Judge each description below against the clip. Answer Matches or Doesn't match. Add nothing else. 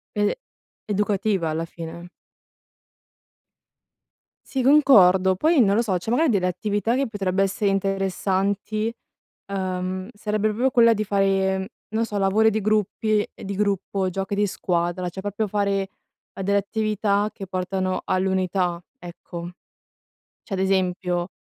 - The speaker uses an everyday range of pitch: Doesn't match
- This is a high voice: Matches